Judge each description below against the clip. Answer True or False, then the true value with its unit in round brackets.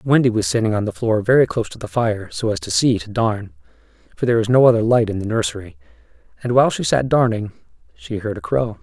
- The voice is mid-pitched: False (105 Hz)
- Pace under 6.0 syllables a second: False (6.4 syllables/s)